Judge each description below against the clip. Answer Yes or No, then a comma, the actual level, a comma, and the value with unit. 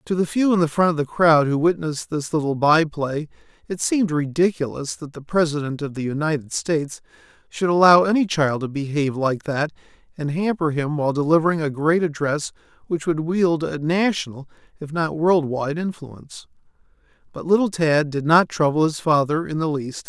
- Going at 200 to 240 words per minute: No, average, 180 wpm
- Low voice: No, medium, 155 Hz